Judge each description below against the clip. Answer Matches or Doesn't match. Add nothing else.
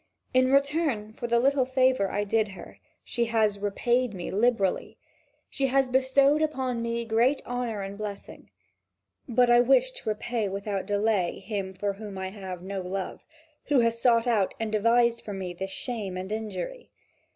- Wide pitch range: Doesn't match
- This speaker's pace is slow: Doesn't match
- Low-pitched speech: Doesn't match